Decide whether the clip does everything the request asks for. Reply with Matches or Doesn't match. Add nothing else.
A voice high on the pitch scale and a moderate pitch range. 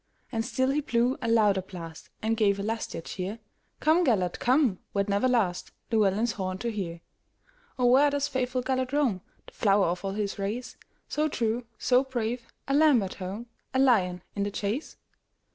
Matches